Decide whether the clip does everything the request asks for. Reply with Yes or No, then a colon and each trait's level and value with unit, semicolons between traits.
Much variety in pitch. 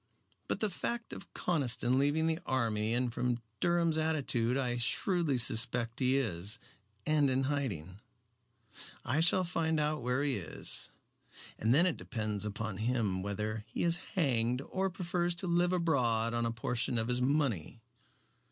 Yes: wide, 5.9 semitones